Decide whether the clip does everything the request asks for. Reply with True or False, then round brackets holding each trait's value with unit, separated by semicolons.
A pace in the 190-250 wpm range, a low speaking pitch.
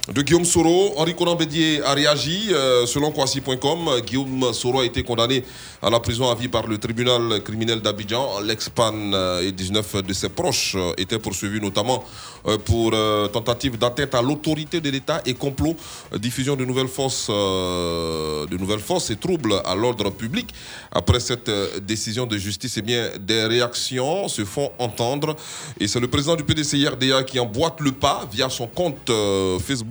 False (160 wpm; 120 Hz)